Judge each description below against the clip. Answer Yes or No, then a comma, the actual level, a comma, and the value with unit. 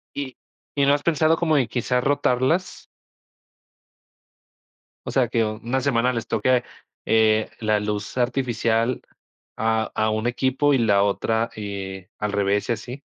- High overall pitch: No, low, 115 Hz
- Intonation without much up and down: No, average, 3.3 semitones